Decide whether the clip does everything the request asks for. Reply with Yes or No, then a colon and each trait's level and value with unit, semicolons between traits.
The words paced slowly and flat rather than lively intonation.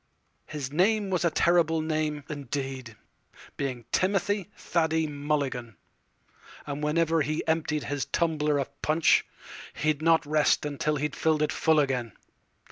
Yes: slow, 125 wpm; narrow, 2.2 semitones